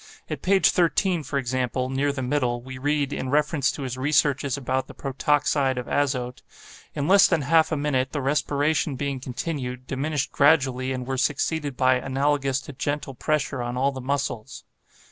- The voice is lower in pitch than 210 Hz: Yes, medium, 140 Hz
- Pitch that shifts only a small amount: Yes, narrow, 2.2 semitones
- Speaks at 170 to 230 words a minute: Yes, average, 175 wpm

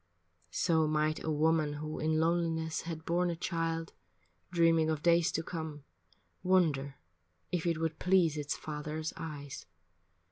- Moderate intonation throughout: No, narrow, 1.5 semitones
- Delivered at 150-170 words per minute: No, average, 140 wpm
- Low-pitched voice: No, medium, 160 Hz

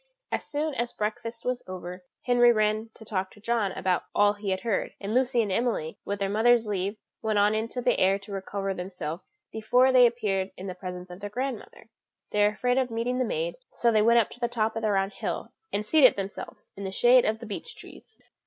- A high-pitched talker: Yes, high, 215 Hz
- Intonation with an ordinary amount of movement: Yes, average, 3.5 semitones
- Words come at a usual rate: No, fast, 225 wpm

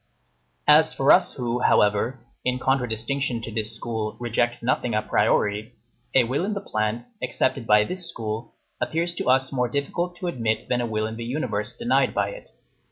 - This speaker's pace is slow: No, average, 180 wpm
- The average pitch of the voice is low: Yes, low, 120 Hz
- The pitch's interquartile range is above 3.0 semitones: Yes, average, 4.2 semitones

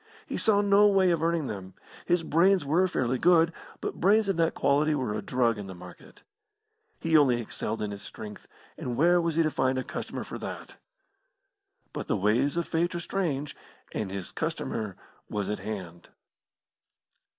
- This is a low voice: No, medium, 145 Hz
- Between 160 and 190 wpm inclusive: Yes, average, 180 wpm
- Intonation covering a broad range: Yes, wide, 8.1 semitones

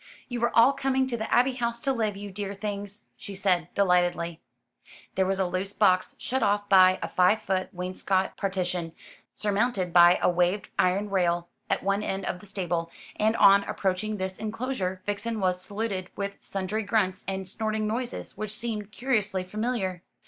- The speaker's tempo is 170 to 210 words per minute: Yes, average, 175 wpm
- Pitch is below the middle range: No, high, 200 Hz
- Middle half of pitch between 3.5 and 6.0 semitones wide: No, average, 2.7 semitones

